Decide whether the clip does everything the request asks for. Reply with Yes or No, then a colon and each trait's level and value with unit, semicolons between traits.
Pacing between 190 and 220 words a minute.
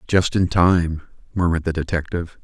No: average, 150 wpm